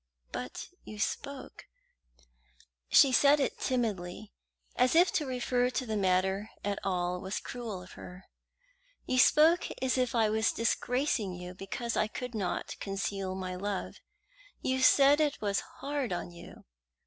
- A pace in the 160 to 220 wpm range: No, average, 150 wpm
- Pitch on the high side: Yes, high, 220 Hz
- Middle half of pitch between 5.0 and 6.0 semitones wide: Yes, wide, 5.4 semitones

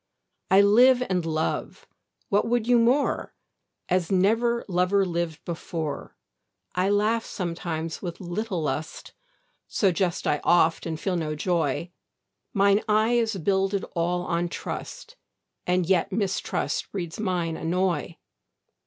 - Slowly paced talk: Yes, slow, 125 wpm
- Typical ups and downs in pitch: Yes, average, 3.5 semitones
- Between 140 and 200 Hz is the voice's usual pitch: Yes, medium, 185 Hz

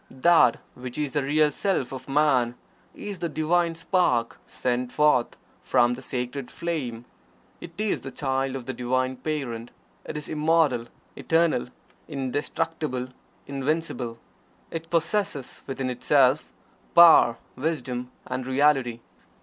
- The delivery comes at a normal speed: No, slow, 125 wpm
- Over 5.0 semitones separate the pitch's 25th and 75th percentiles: No, average, 4.1 semitones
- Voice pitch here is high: No, low, 135 Hz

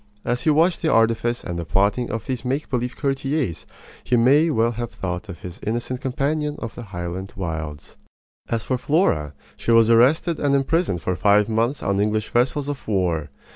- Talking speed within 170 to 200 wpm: Yes, average, 185 wpm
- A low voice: Yes, low, 115 Hz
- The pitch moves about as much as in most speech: No, wide, 5.8 semitones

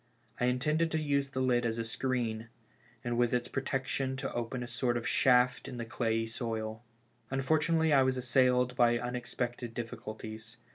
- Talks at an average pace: Yes, average, 180 wpm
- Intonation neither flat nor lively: No, narrow, 2.1 semitones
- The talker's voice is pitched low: Yes, low, 125 Hz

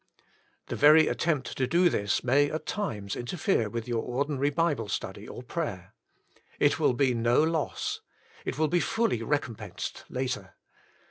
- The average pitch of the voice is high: No, medium, 140 Hz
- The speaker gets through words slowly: No, average, 155 wpm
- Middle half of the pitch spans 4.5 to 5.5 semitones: Yes, average, 4.8 semitones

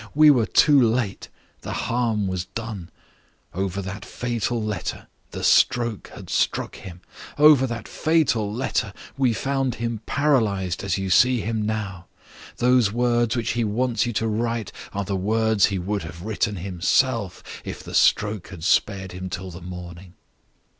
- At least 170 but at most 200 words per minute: No, average, 160 wpm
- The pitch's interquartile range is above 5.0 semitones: No, average, 3.8 semitones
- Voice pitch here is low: Yes, low, 110 Hz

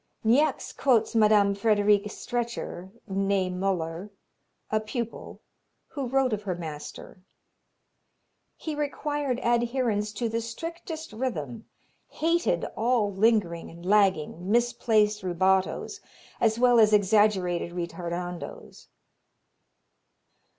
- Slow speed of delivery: Yes, slow, 95 wpm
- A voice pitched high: Yes, high, 210 Hz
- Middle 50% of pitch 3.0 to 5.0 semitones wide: Yes, average, 4.3 semitones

